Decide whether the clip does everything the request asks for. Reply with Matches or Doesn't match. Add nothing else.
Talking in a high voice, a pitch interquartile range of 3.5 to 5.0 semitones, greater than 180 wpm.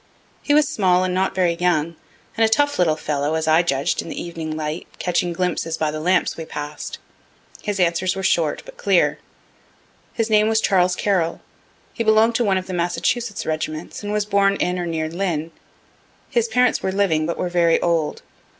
Doesn't match